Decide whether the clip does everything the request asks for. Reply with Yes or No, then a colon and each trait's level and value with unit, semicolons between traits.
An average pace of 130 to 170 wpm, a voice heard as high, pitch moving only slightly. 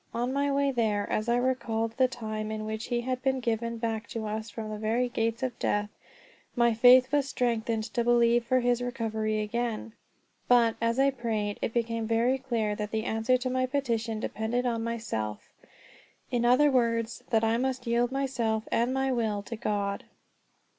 No: average, 185 wpm; high, 235 Hz; narrow, 2.2 semitones